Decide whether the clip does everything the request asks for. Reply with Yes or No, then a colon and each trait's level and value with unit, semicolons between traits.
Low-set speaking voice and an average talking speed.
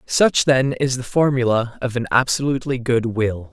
Yes: low, 125 Hz; average, 170 wpm